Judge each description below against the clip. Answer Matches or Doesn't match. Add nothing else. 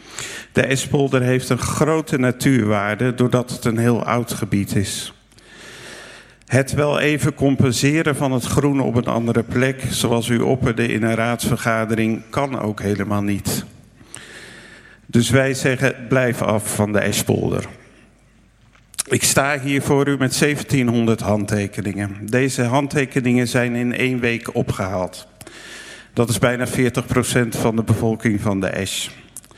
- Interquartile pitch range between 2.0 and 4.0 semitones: Matches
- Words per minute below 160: Matches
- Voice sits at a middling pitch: Doesn't match